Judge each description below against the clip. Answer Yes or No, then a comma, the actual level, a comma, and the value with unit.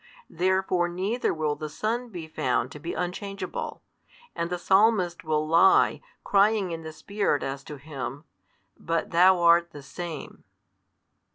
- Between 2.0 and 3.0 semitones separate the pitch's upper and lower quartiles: No, average, 3.5 semitones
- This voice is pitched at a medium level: Yes, medium, 175 Hz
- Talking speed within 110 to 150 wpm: Yes, average, 145 wpm